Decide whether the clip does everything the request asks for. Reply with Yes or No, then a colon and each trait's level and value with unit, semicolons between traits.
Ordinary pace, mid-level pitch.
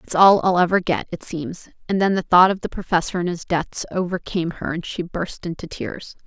No: fast, 230 wpm; medium, 175 Hz